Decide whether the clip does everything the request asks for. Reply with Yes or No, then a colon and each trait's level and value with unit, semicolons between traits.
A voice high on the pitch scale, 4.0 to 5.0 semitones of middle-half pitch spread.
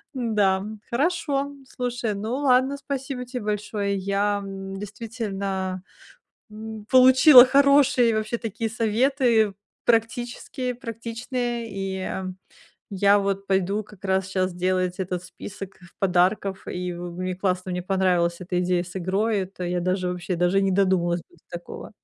Yes: high, 200 Hz; average, 4.3 semitones